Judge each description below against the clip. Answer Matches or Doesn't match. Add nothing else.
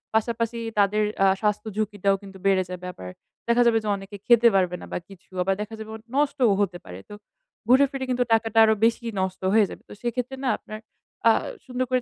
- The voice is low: Doesn't match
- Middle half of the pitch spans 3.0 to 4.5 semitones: Matches